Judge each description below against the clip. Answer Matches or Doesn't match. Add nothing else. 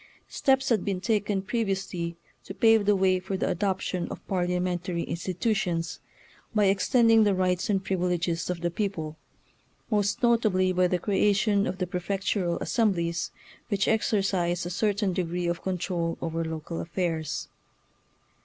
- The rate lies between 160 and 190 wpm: Doesn't match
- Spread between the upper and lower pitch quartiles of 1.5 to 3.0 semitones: Matches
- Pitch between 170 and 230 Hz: Matches